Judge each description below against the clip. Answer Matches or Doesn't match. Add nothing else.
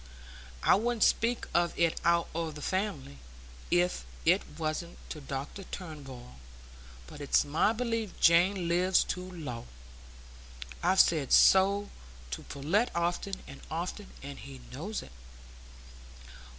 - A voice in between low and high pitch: Matches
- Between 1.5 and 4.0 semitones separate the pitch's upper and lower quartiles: Doesn't match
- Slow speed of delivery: Matches